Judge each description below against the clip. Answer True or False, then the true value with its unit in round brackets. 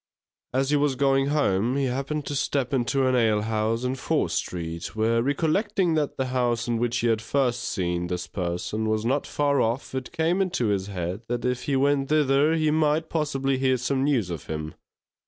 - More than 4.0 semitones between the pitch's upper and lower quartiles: True (4.4 semitones)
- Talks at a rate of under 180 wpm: False (195 wpm)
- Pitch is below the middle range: True (130 Hz)